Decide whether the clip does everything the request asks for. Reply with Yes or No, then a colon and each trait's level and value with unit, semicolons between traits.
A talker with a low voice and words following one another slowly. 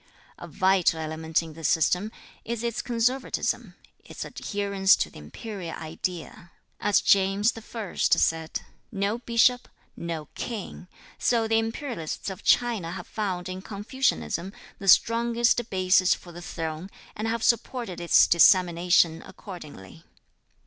No: high, 195 Hz; slow, 130 wpm